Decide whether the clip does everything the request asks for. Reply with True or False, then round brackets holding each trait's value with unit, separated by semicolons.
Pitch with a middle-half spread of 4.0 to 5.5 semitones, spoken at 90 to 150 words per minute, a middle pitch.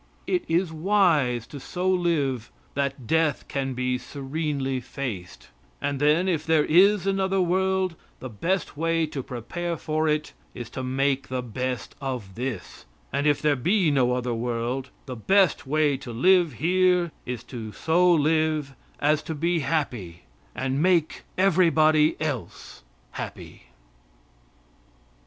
True (4.8 semitones; 140 wpm; 150 Hz)